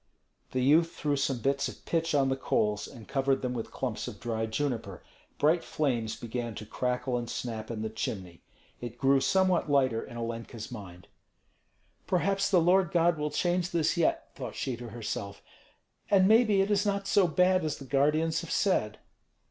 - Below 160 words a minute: No, average, 180 wpm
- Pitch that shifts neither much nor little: No, wide, 6.6 semitones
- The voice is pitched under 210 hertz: Yes, low, 135 Hz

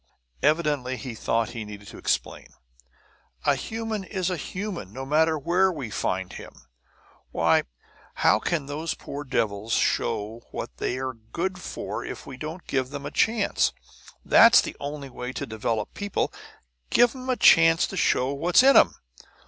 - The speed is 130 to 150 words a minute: No, average, 160 wpm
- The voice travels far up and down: Yes, wide, 7.3 semitones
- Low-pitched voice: No, medium, 145 Hz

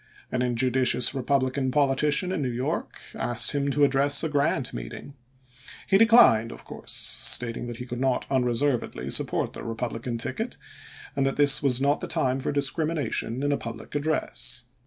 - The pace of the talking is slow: No, average, 170 wpm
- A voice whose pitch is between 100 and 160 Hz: Yes, low, 135 Hz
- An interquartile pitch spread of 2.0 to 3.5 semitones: Yes, average, 2.8 semitones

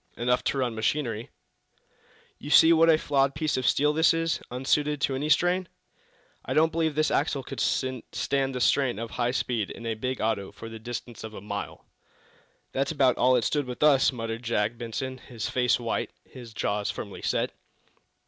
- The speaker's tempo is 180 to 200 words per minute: Yes, average, 185 wpm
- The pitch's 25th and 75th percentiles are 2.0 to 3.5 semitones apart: No, average, 4.3 semitones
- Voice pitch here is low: Yes, low, 130 Hz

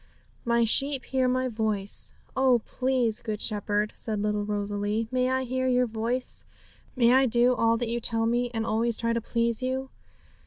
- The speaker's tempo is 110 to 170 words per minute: No, average, 180 wpm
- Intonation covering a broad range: No, narrow, 2.6 semitones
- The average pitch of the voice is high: Yes, high, 235 Hz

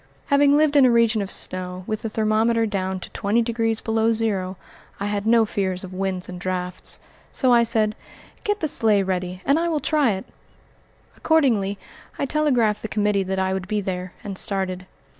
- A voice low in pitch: No, high, 210 Hz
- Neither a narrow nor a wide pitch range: Yes, average, 3.7 semitones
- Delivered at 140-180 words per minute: No, average, 190 wpm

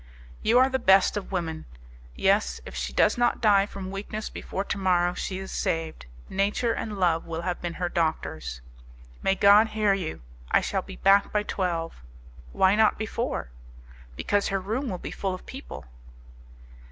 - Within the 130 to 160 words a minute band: No, average, 175 wpm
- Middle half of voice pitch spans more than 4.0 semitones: No, average, 3.5 semitones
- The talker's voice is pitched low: No, high, 195 Hz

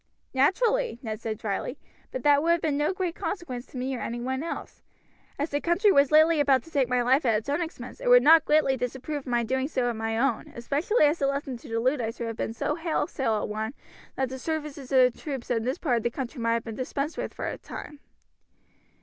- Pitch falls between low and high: No, very high, 265 Hz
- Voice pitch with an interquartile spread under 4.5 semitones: Yes, average, 4.1 semitones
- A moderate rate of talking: No, fast, 250 wpm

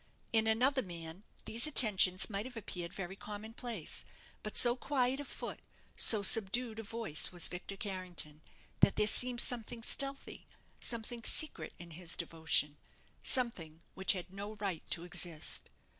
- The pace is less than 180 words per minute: Yes, average, 150 wpm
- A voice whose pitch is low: No, high, 210 Hz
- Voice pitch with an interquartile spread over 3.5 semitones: Yes, average, 5.0 semitones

